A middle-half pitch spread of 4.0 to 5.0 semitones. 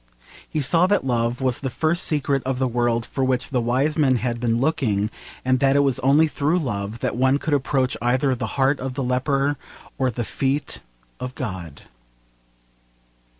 No: average, 2.7 semitones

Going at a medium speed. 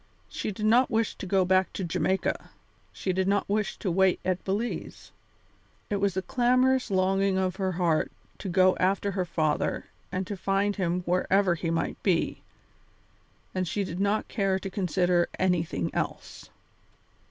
Yes: average, 165 wpm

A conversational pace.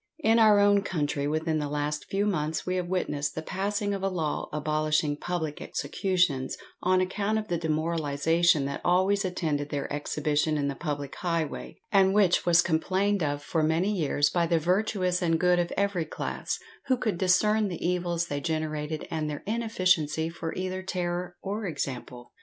Yes: average, 175 wpm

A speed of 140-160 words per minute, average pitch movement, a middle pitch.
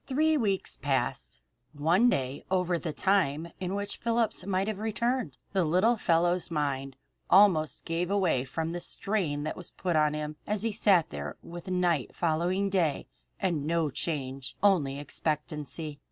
Yes: average, 155 wpm; average, 4.6 semitones; medium, 170 Hz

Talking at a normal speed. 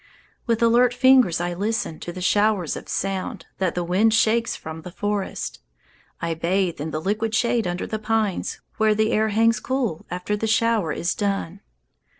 Yes: average, 175 wpm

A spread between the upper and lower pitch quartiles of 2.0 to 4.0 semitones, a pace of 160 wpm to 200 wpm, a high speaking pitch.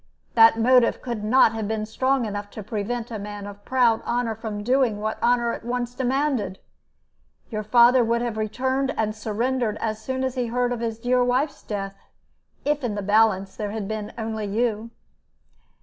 Yes: narrow, 2.6 semitones; average, 180 wpm; high, 225 Hz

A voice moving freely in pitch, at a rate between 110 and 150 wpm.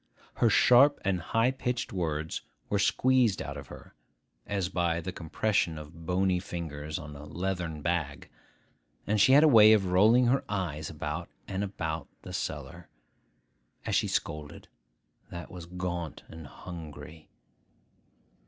No: average, 4.4 semitones; average, 145 wpm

